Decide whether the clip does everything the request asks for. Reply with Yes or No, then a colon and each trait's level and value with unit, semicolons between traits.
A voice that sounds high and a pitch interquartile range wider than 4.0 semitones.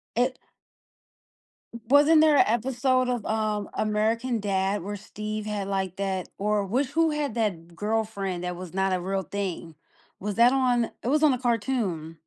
Yes: high, 215 Hz; average, 4.4 semitones